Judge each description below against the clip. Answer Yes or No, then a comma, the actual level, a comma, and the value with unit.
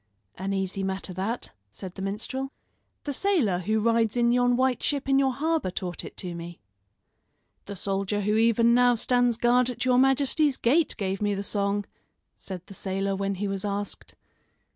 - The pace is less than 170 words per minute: No, average, 180 wpm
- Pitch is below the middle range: No, high, 210 Hz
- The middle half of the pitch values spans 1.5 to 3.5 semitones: No, average, 4.2 semitones